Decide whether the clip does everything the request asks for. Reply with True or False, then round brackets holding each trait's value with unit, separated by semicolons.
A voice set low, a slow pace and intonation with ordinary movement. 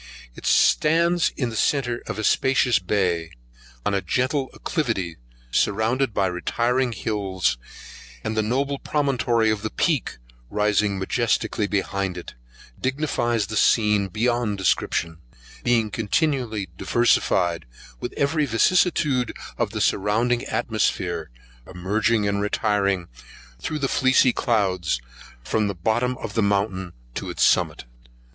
True (110 Hz; 125 wpm; 4.2 semitones)